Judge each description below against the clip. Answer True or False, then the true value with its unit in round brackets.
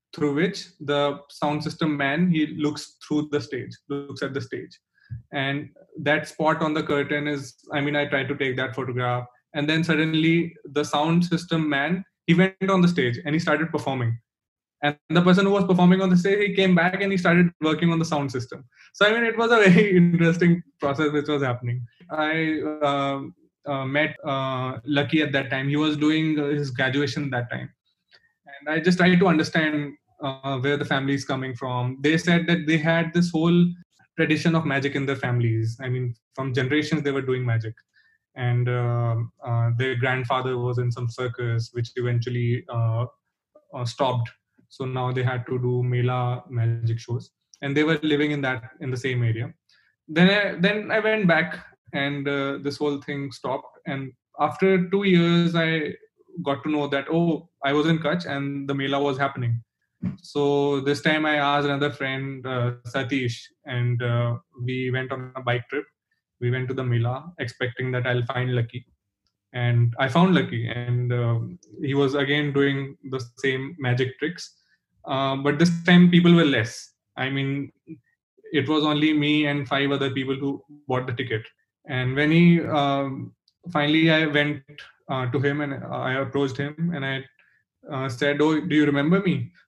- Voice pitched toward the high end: False (140 Hz)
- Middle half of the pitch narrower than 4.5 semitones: True (3.6 semitones)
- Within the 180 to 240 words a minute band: True (185 wpm)